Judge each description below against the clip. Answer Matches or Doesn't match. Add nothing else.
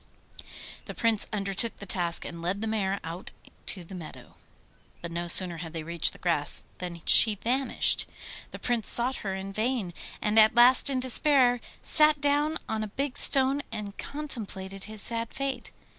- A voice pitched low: Doesn't match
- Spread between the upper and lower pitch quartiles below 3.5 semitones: Doesn't match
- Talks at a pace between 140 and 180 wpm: Matches